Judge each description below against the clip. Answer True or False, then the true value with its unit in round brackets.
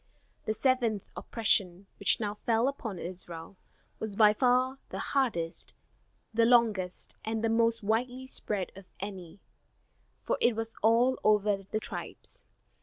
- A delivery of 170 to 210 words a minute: False (135 wpm)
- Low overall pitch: False (220 Hz)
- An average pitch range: True (3.2 semitones)